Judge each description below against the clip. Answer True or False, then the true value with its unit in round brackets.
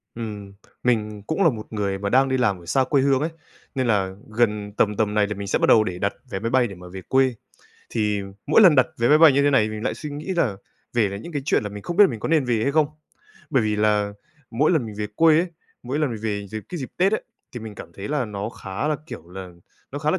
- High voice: False (115 Hz)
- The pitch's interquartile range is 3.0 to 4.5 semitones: False (5.4 semitones)